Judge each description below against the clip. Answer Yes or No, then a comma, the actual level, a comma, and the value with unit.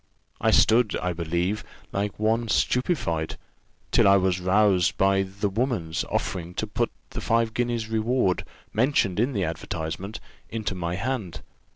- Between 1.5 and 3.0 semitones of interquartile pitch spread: No, average, 4.1 semitones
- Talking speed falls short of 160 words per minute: Yes, average, 145 wpm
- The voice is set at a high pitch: No, low, 100 Hz